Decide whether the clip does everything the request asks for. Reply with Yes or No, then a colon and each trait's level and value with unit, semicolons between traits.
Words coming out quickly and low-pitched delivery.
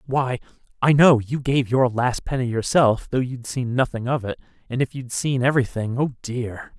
No: average, 195 wpm; low, 125 Hz